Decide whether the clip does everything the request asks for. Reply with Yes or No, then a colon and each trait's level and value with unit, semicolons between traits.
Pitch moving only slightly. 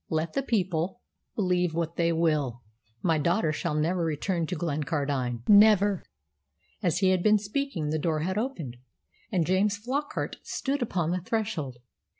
No: average, 4.7 semitones